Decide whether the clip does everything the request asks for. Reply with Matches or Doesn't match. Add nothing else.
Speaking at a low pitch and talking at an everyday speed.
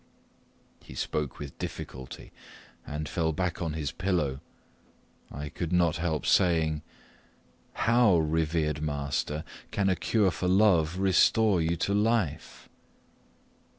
Doesn't match